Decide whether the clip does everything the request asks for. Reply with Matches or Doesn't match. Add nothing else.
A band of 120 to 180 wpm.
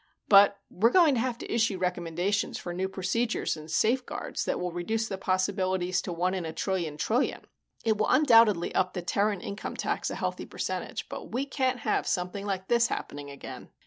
Doesn't match